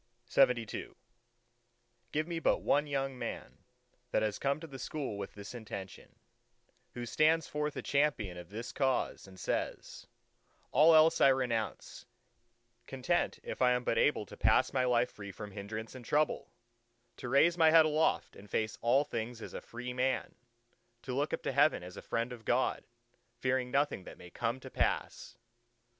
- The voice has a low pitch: Yes, low, 125 Hz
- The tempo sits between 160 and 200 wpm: Yes, average, 175 wpm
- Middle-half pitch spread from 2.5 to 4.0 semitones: No, average, 4.6 semitones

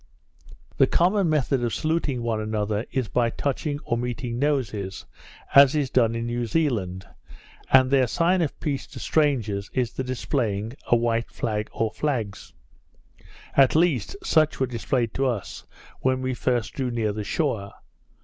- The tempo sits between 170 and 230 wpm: No, average, 160 wpm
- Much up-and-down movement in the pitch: No, average, 3.8 semitones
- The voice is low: Yes, low, 125 Hz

